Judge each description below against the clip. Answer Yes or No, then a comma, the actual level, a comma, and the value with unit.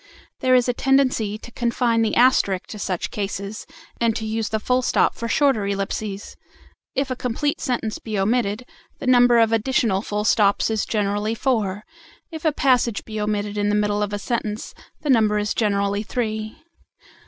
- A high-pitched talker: Yes, high, 220 Hz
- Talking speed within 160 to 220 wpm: Yes, average, 175 wpm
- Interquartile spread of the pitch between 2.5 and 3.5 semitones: Yes, average, 2.9 semitones